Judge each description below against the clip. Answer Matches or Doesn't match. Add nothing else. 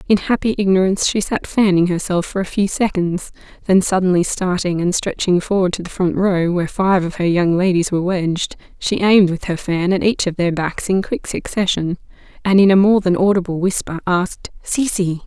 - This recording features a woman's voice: Matches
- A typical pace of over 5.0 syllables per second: Matches